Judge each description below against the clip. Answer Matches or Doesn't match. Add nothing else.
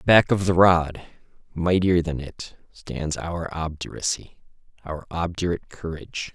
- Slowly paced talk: Matches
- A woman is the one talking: Doesn't match